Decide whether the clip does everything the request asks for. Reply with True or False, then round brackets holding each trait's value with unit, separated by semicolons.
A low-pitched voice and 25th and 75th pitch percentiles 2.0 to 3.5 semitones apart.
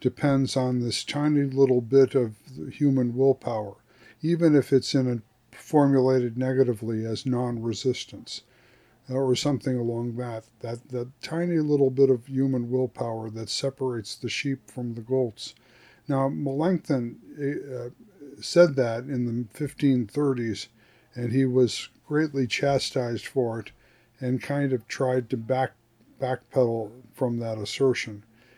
True (130 Hz; 2.5 semitones)